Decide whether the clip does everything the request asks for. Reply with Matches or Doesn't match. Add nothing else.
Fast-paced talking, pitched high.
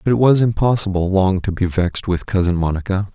Doesn't match